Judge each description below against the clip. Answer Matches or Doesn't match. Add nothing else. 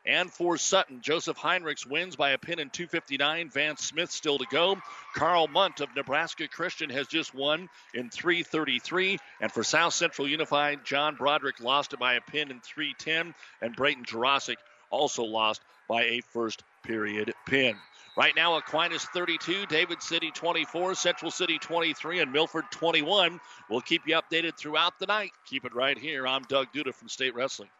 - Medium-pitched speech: Matches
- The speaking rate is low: Doesn't match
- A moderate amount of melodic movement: Matches